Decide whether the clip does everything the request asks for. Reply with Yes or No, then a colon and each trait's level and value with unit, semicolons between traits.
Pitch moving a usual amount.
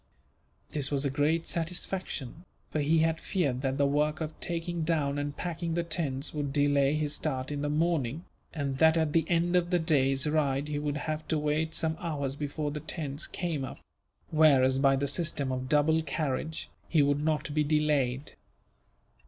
No: narrow, 2.3 semitones